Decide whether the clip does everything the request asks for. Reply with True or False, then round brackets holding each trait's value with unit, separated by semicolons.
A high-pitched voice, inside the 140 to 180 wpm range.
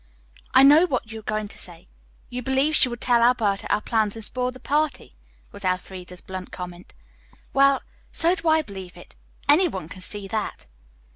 False (225 Hz; 190 wpm)